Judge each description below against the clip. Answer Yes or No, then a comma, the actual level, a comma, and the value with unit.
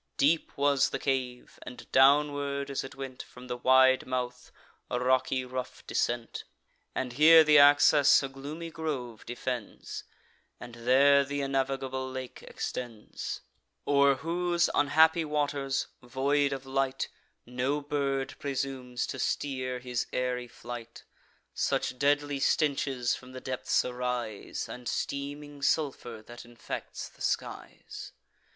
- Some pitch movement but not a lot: No, narrow, 2.2 semitones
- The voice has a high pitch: No, low, 135 Hz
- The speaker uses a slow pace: Yes, slow, 125 wpm